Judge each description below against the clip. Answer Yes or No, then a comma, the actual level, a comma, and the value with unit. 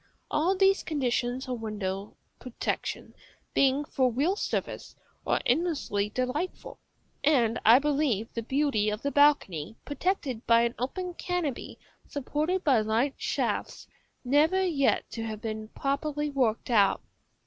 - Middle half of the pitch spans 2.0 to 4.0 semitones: No, average, 4.8 semitones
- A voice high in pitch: Yes, very high, 265 Hz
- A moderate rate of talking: No, slow, 130 wpm